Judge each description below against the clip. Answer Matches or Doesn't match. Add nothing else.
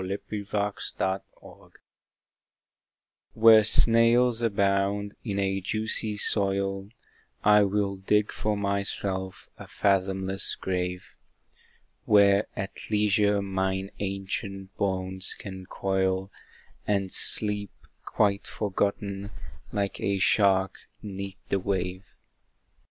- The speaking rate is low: Matches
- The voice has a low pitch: Matches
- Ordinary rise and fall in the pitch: Doesn't match